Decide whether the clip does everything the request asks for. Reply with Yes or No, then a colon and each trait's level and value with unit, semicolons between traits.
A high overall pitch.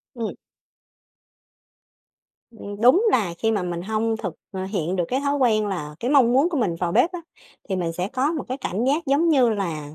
Yes: high, 225 Hz